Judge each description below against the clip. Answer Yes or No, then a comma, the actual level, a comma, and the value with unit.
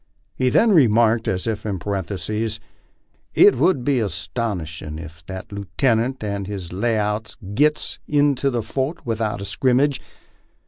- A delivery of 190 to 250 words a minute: No, average, 140 wpm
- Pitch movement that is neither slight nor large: Yes, average, 4.7 semitones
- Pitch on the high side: No, low, 110 Hz